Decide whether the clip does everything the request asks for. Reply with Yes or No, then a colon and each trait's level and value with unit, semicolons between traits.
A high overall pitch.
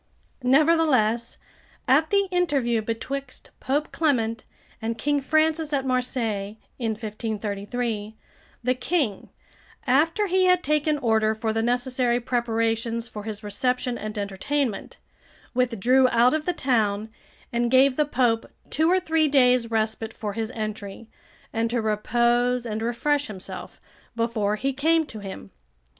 Yes: high, 240 Hz